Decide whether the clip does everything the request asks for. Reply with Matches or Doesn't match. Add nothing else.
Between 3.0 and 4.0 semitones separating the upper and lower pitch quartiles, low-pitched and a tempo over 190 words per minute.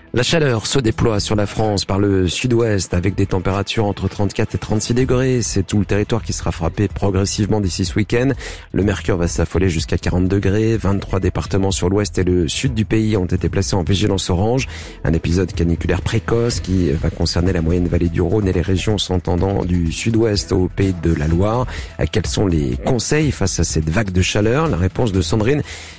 Matches